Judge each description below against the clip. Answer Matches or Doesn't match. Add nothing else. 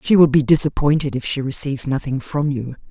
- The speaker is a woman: Matches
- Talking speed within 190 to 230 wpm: Matches